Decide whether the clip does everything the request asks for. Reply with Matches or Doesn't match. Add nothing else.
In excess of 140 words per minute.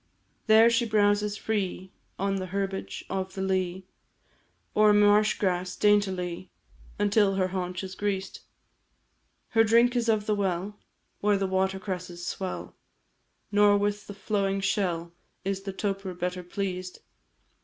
Doesn't match